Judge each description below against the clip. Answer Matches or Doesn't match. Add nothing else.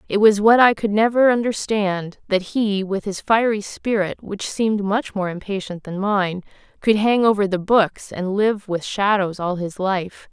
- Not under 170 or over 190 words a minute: Matches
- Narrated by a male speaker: Doesn't match